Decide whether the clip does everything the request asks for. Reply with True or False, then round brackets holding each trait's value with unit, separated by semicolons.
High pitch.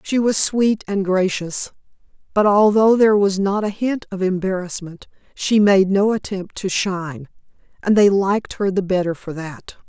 True (195 Hz)